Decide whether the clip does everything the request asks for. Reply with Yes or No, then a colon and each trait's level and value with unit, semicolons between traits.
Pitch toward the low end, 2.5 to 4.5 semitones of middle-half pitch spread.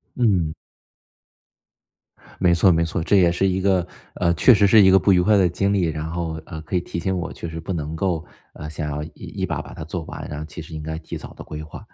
Yes: very low, 85 Hz; average, 3.1 semitones